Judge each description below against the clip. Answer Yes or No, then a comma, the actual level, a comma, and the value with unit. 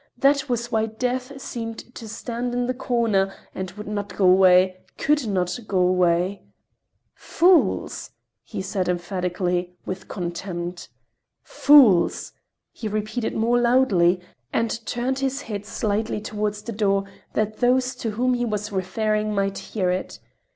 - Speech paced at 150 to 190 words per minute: No, average, 140 wpm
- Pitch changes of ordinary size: Yes, average, 4.4 semitones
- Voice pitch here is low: No, high, 215 Hz